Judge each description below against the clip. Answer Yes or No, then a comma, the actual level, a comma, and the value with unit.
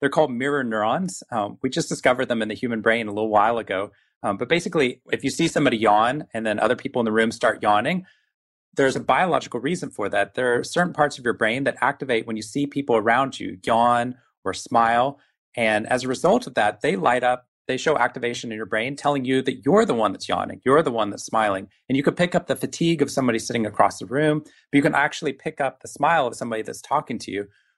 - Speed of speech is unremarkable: No, fast, 245 wpm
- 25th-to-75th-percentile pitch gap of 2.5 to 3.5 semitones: No, average, 4.0 semitones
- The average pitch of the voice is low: Yes, low, 125 Hz